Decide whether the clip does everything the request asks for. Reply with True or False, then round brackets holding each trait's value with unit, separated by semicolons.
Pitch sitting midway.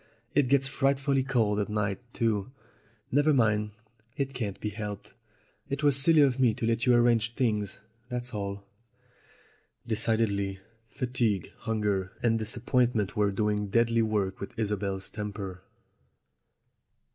False (110 Hz)